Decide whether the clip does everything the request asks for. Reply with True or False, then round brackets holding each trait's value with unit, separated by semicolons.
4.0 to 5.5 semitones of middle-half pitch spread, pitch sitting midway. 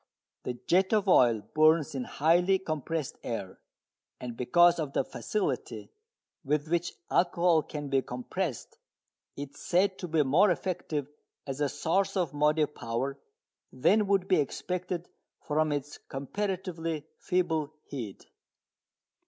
True (4.4 semitones; 155 Hz)